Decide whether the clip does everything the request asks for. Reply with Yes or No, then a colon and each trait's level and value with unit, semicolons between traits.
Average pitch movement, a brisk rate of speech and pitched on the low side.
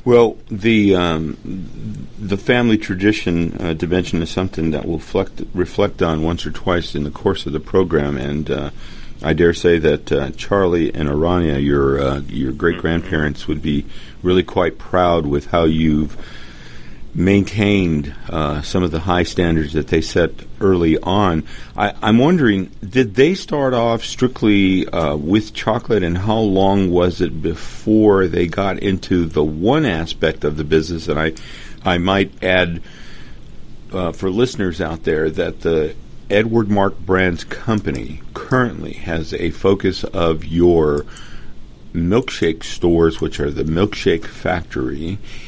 No: average, 3.9 semitones; average, 150 wpm; very low, 85 Hz